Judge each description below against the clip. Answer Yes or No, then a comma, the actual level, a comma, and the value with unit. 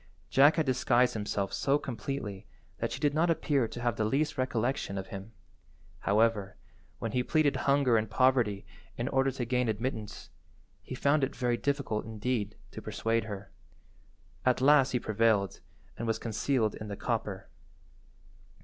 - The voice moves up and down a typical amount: Yes, average, 3.8 semitones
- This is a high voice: No, low, 120 Hz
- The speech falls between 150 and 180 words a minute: Yes, average, 160 wpm